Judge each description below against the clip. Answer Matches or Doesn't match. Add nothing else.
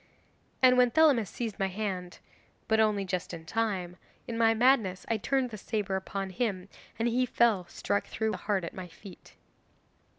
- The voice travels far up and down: Doesn't match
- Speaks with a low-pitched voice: Doesn't match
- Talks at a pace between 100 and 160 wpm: Doesn't match